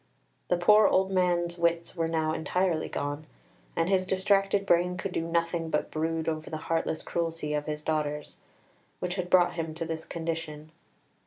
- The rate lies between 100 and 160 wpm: No, average, 170 wpm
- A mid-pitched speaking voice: Yes, medium, 165 Hz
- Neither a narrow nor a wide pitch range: No, narrow, 2.2 semitones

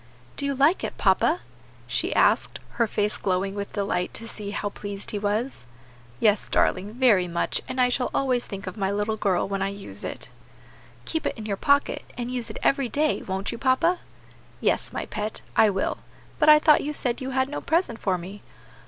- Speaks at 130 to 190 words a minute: No, fast, 205 wpm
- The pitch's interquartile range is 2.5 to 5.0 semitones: Yes, average, 4.7 semitones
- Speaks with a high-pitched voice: Yes, high, 220 Hz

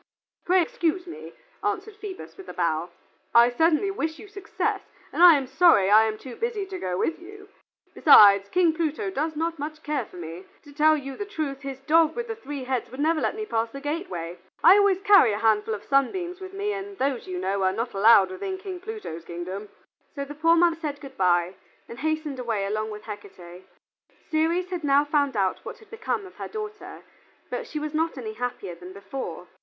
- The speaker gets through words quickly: Yes, fast, 210 wpm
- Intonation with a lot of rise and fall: Yes, wide, 9.0 semitones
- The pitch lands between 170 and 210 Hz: No, very high, 295 Hz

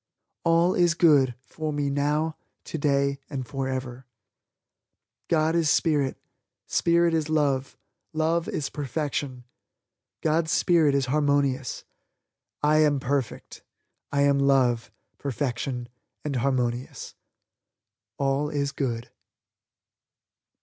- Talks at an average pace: No, slow, 100 wpm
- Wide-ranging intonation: No, average, 2.7 semitones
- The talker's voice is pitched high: No, medium, 140 Hz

